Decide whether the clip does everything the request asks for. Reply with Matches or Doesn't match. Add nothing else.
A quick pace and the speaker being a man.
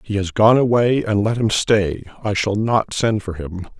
Matches